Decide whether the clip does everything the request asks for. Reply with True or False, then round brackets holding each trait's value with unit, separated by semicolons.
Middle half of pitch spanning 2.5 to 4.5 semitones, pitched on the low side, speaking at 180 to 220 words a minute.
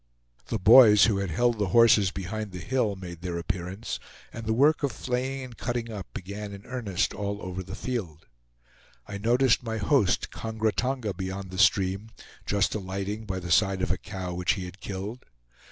True (3.7 semitones; 100 Hz; 185 wpm)